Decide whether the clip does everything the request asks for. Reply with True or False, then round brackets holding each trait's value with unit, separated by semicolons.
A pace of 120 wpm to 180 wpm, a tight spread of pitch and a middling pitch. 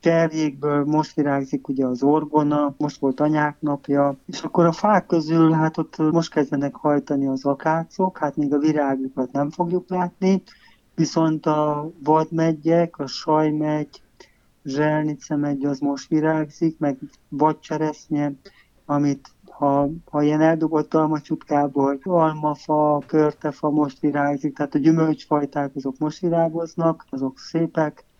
True (125 wpm; 1.8 semitones; 150 Hz)